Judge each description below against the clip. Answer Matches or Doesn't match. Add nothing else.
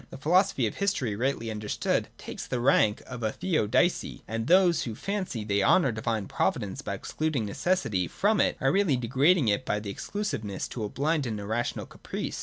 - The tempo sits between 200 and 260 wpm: Doesn't match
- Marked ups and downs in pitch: Matches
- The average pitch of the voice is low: Matches